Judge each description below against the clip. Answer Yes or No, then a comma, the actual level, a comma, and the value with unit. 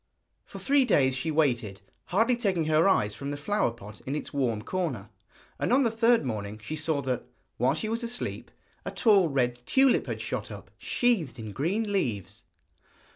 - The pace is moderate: Yes, average, 180 wpm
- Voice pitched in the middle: Yes, medium, 155 Hz